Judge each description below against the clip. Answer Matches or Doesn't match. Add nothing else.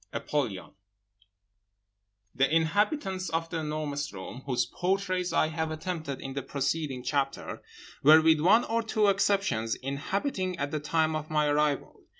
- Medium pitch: Matches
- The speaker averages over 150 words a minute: Doesn't match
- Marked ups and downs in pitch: Doesn't match